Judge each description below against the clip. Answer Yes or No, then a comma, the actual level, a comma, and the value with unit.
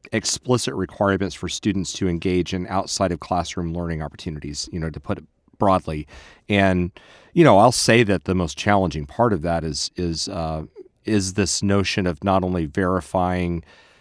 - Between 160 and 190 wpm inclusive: Yes, average, 170 wpm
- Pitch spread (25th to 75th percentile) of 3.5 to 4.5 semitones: No, average, 2.9 semitones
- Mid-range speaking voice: No, very low, 90 Hz